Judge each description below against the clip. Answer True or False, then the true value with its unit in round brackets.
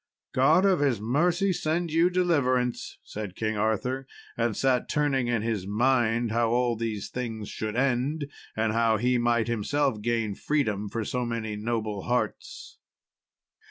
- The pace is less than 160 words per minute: True (150 wpm)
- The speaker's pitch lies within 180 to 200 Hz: False (120 Hz)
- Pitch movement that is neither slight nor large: True (3.5 semitones)